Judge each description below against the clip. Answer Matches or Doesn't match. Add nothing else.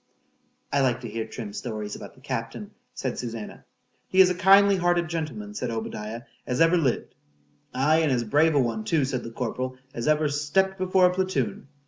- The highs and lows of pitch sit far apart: Matches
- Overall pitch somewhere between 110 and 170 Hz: Matches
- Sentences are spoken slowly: Doesn't match